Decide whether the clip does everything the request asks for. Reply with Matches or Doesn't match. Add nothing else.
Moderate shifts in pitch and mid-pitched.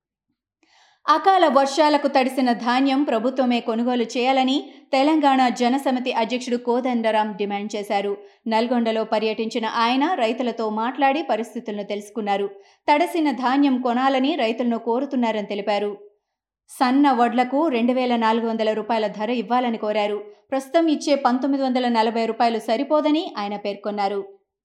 Doesn't match